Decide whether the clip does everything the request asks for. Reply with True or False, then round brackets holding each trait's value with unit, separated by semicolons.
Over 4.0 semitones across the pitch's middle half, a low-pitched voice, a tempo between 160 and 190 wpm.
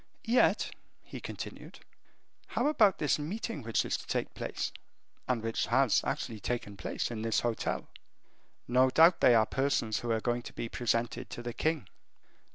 True (4.4 semitones; 120 Hz; 165 wpm)